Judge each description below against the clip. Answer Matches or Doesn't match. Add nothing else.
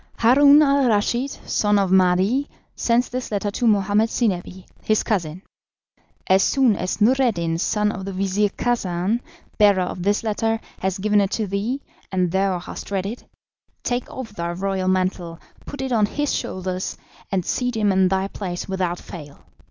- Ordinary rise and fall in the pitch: Matches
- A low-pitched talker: Doesn't match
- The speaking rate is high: Doesn't match